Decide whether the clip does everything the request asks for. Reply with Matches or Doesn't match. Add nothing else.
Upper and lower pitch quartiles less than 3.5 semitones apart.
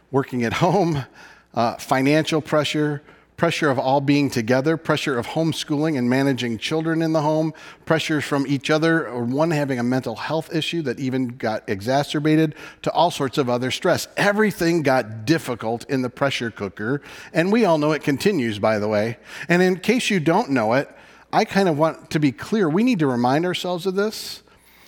Doesn't match